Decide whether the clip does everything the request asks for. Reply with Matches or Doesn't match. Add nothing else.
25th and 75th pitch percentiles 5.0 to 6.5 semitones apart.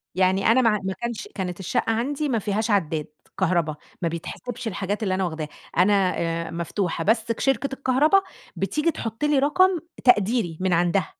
Matches